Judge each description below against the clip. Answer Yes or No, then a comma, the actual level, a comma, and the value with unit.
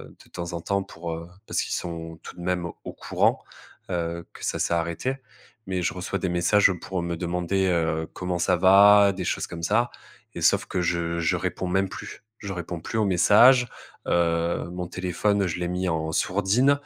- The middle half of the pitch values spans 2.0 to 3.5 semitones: Yes, narrow, 2.4 semitones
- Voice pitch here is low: Yes, very low, 90 Hz